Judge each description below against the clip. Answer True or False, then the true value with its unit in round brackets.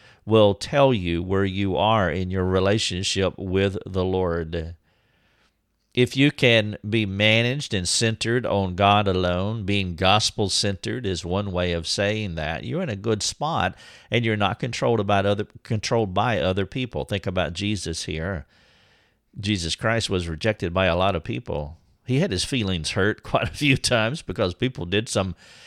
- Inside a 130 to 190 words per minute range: True (170 wpm)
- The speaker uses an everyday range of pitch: True (3.3 semitones)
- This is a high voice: False (100 Hz)